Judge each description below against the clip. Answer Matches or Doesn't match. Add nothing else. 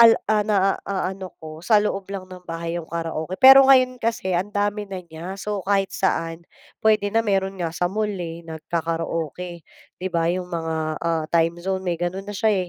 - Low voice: Doesn't match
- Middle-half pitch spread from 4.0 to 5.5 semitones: Doesn't match